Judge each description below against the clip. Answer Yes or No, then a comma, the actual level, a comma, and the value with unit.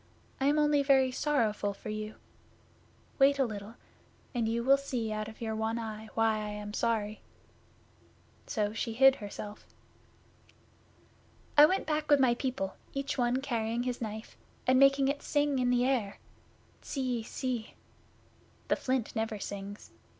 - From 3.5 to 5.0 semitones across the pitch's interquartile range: Yes, average, 3.9 semitones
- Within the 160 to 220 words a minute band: No, average, 150 wpm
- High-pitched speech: Yes, high, 240 Hz